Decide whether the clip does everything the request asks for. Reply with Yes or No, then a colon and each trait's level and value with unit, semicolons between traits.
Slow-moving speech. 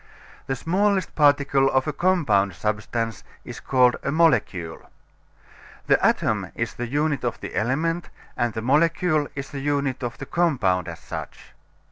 No: average, 150 wpm